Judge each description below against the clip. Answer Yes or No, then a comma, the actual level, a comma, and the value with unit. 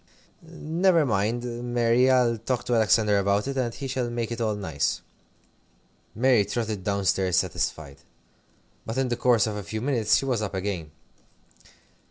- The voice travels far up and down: No, average, 3.9 semitones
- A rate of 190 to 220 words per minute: No, average, 165 wpm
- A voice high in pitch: No, low, 115 Hz